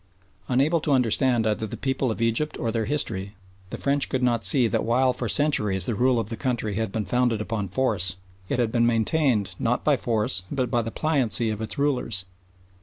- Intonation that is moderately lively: Yes, average, 3.2 semitones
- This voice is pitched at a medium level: No, low, 120 Hz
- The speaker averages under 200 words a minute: No, fast, 205 wpm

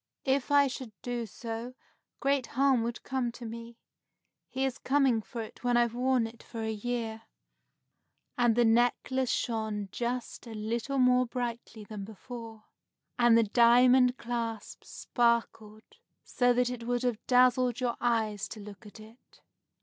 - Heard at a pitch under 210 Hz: No, high, 240 Hz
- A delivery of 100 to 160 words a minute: Yes, average, 155 wpm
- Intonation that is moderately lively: No, narrow, 1.9 semitones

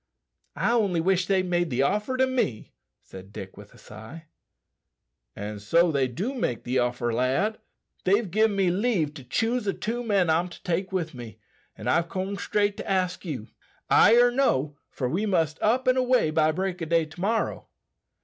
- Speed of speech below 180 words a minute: No, average, 190 wpm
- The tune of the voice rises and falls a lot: Yes, wide, 6.7 semitones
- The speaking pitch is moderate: Yes, medium, 180 Hz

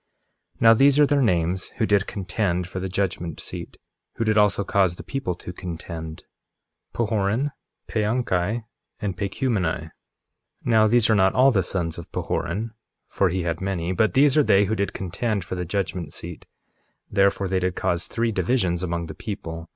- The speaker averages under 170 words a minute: No, average, 180 wpm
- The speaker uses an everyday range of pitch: Yes, average, 3.9 semitones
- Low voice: Yes, very low, 95 Hz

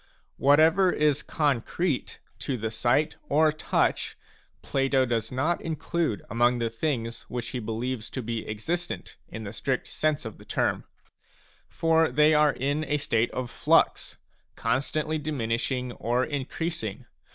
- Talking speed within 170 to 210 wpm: No, average, 140 wpm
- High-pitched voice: No, low, 135 Hz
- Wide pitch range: No, average, 4.8 semitones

